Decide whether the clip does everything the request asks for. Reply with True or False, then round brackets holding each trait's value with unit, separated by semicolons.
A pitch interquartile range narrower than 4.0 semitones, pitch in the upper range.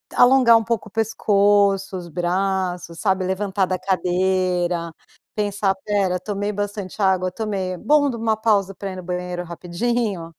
True (2.6 semitones; 195 Hz)